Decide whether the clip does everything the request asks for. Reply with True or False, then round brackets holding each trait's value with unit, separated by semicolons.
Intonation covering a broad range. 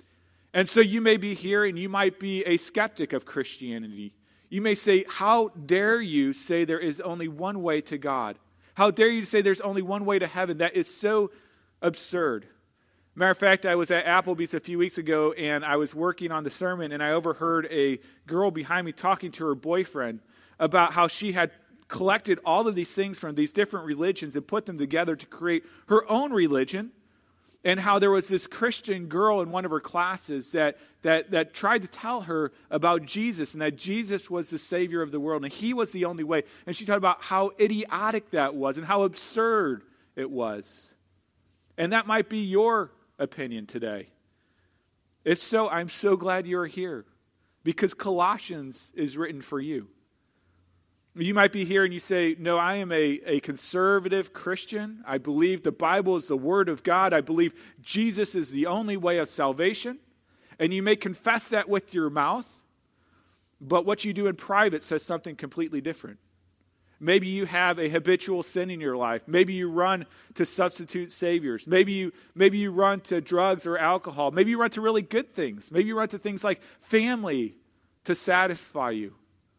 False (4.7 semitones)